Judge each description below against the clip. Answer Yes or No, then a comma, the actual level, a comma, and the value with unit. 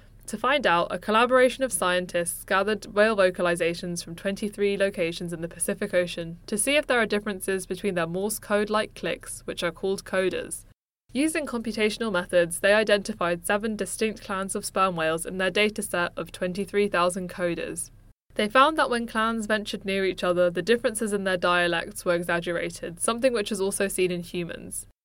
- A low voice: No, high, 195 Hz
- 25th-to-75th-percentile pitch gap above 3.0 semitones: Yes, average, 3.6 semitones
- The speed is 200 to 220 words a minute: No, average, 175 wpm